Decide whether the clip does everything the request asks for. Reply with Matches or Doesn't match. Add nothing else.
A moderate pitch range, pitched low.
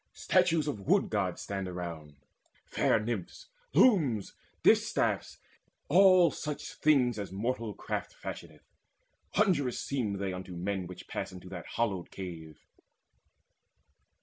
Doesn't match